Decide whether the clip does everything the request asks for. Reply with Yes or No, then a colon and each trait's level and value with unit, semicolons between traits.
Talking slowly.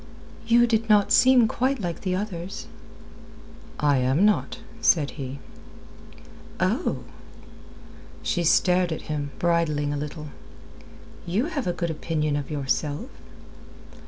Yes: slow, 120 wpm